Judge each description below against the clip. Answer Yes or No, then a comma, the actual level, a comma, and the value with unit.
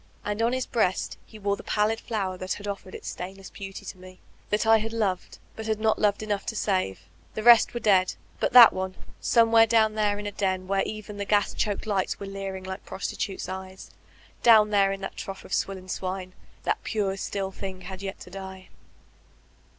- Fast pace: Yes, fast, 210 wpm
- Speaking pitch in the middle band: No, high, 200 Hz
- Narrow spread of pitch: Yes, narrow, 2.2 semitones